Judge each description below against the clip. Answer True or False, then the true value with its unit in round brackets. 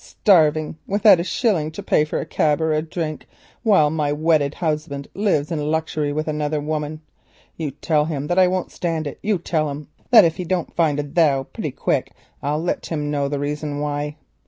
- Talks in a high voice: False (155 Hz)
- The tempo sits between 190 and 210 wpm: True (205 wpm)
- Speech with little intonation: True (2.2 semitones)